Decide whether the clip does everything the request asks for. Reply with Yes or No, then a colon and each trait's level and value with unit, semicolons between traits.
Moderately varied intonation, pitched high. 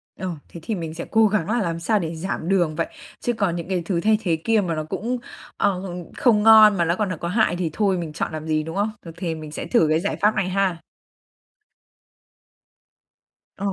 No: average, 4.1 semitones; medium, 180 Hz